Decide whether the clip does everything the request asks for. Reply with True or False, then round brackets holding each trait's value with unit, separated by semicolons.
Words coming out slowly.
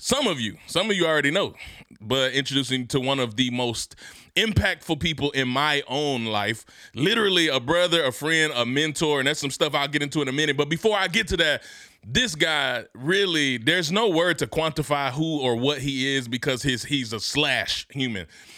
False (205 wpm)